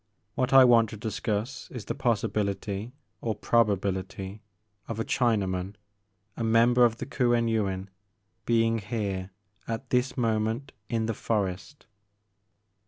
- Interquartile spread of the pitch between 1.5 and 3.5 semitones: Yes, average, 2.8 semitones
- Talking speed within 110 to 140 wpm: Yes, slow, 135 wpm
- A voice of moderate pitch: No, low, 110 Hz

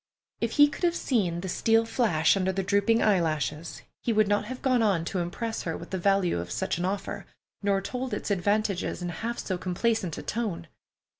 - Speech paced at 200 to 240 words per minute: Yes, fast, 205 wpm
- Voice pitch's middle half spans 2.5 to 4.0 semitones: No, average, 4.4 semitones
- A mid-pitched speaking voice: No, high, 200 Hz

